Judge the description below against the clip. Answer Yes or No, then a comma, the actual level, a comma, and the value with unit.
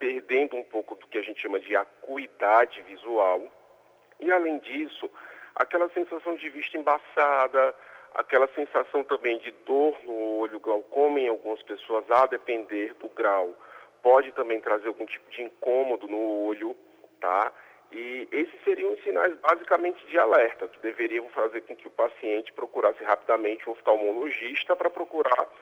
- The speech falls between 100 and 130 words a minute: No, average, 150 wpm